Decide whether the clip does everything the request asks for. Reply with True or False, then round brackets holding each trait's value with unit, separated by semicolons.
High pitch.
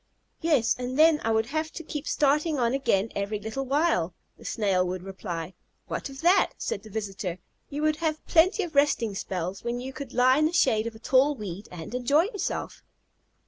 True (250 Hz)